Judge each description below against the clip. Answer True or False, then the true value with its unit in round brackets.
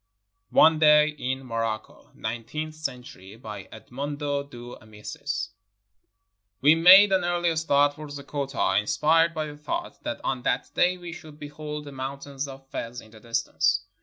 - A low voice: False (145 Hz)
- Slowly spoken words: False (155 wpm)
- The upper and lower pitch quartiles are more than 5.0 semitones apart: False (4.2 semitones)